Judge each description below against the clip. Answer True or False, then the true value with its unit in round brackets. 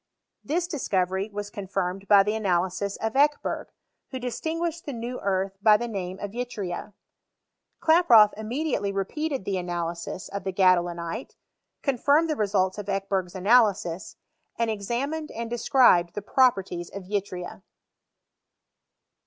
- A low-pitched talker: False (205 Hz)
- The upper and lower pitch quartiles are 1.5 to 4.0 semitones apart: False (4.7 semitones)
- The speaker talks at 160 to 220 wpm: False (135 wpm)